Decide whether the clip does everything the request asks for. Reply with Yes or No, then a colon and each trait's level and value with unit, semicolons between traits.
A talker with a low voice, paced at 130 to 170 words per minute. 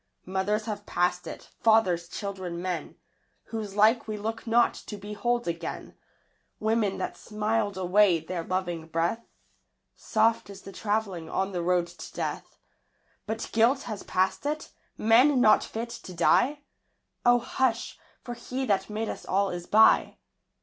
No: high, 210 Hz; average, 150 wpm